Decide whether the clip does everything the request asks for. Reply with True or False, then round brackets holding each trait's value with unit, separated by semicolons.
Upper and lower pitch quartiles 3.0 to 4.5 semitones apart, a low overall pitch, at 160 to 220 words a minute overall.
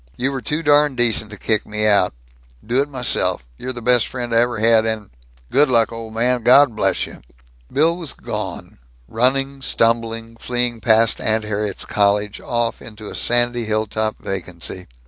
False (2.5 semitones; 115 Hz; 165 wpm)